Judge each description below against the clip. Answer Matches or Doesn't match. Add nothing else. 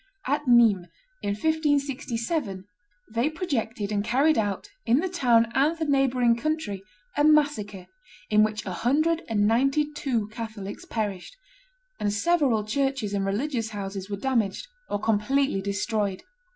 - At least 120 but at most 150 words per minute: Matches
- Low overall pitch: Doesn't match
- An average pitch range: Doesn't match